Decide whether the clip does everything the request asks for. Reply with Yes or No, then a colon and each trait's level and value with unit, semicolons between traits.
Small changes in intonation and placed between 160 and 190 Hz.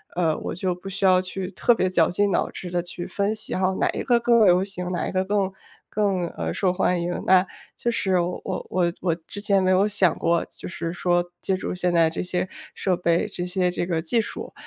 Yes: narrow, 1.8 semitones; medium, 185 Hz